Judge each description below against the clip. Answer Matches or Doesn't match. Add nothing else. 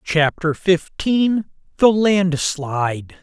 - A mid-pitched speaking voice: Matches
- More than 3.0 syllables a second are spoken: Doesn't match